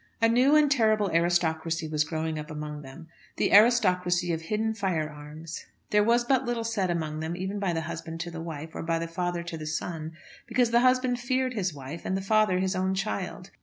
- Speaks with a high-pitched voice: No, medium, 180 Hz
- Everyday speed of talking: No, fast, 210 wpm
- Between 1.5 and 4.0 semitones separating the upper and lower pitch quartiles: No, average, 5.3 semitones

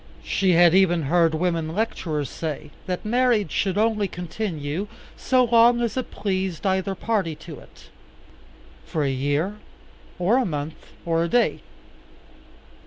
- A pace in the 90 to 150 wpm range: Yes, average, 140 wpm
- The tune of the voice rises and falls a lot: No, average, 4.8 semitones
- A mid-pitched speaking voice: Yes, medium, 180 Hz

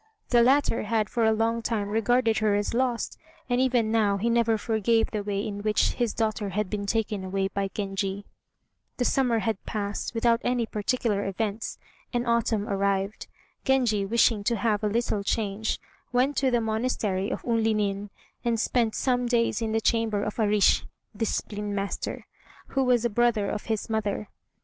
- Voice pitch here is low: No, high, 220 Hz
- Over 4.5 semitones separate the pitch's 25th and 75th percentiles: No, narrow, 2.4 semitones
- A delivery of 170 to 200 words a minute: Yes, average, 175 wpm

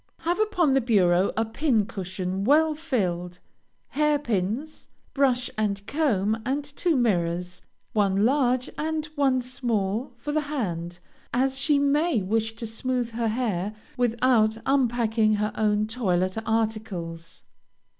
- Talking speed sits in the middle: No, slow, 130 wpm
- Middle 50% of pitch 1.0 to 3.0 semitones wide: No, average, 5.2 semitones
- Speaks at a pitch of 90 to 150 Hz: No, high, 230 Hz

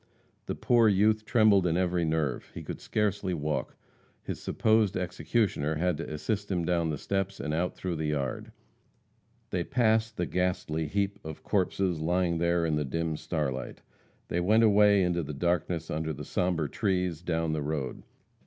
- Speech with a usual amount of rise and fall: Yes, average, 4.0 semitones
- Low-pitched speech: Yes, very low, 90 Hz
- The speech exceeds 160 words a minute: Yes, average, 170 wpm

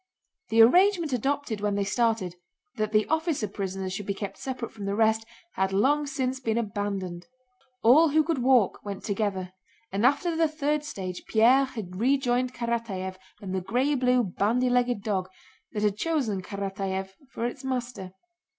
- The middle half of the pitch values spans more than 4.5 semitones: Yes, average, 4.9 semitones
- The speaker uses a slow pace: No, average, 165 wpm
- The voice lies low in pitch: No, high, 225 Hz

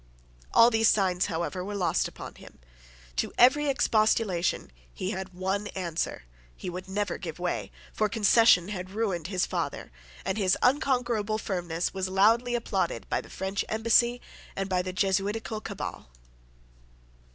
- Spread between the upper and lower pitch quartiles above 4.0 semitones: No, average, 3.4 semitones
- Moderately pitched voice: No, high, 195 Hz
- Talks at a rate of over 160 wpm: No, average, 145 wpm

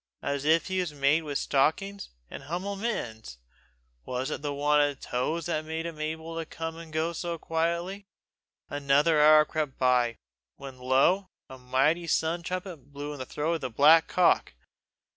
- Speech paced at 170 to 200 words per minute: Yes, average, 175 wpm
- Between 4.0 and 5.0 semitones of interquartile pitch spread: No, average, 3.2 semitones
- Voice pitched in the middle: Yes, medium, 155 Hz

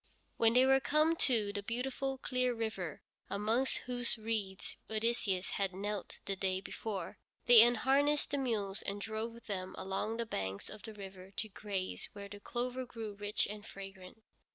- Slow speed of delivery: No, average, 165 wpm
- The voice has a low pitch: No, high, 220 Hz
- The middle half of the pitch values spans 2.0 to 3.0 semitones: No, average, 3.6 semitones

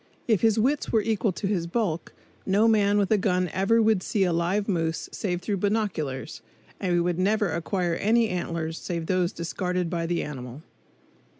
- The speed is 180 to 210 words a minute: Yes, average, 185 wpm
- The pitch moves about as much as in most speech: Yes, average, 3.7 semitones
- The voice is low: No, medium, 185 Hz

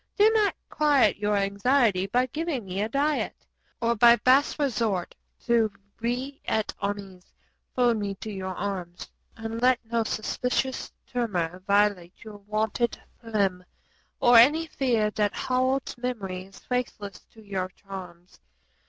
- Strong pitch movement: No, average, 4.1 semitones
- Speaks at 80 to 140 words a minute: Yes, slow, 135 wpm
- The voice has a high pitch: Yes, high, 220 Hz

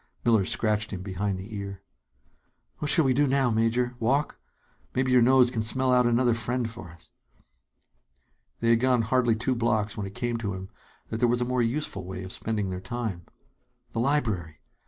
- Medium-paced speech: Yes, average, 190 wpm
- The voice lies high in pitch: No, low, 115 Hz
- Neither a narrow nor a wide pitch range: Yes, average, 3.7 semitones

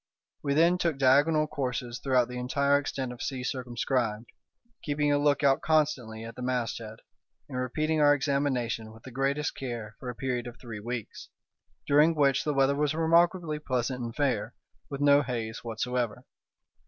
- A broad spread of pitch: No, average, 3.2 semitones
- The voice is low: Yes, low, 130 Hz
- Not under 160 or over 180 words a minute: Yes, average, 165 wpm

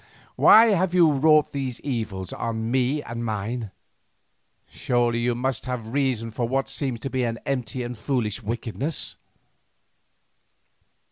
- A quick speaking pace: No, average, 140 wpm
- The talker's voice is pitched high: No, low, 125 Hz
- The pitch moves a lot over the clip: No, average, 2.9 semitones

